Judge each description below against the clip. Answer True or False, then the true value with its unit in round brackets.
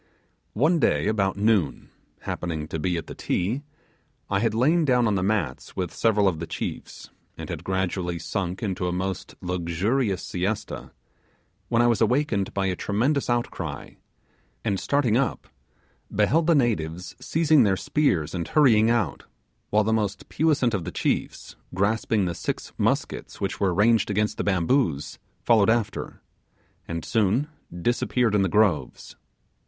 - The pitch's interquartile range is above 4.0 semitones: True (4.7 semitones)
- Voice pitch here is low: True (105 Hz)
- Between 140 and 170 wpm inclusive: True (155 wpm)